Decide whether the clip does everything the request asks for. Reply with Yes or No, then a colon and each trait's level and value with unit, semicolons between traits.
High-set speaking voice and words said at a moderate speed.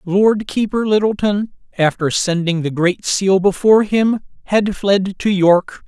Yes: high, 195 Hz; average, 145 wpm